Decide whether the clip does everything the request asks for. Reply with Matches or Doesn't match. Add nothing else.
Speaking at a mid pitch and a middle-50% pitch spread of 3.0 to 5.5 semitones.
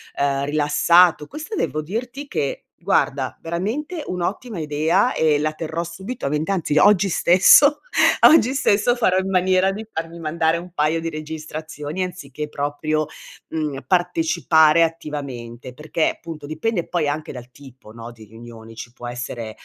Matches